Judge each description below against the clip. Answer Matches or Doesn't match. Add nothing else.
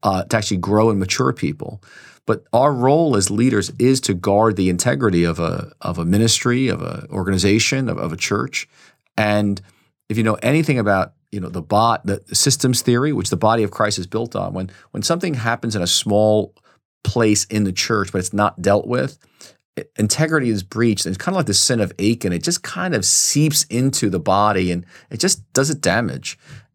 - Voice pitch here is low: Matches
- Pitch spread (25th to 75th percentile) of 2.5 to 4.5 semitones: Matches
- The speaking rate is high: Matches